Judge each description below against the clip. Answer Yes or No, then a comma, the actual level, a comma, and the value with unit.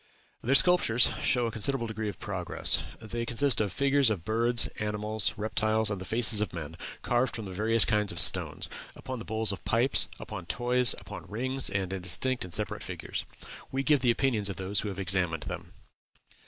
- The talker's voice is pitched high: No, low, 110 Hz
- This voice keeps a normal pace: Yes, average, 190 wpm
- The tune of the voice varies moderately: Yes, average, 3.4 semitones